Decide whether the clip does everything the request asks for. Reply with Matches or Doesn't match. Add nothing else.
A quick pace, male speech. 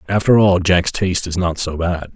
Matches